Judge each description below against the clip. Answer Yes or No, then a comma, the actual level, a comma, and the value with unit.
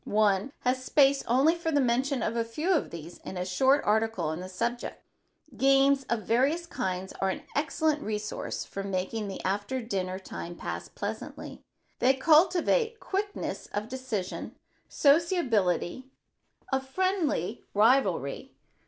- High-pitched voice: Yes, high, 245 Hz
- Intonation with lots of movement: Yes, wide, 6.4 semitones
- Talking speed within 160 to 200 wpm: No, average, 140 wpm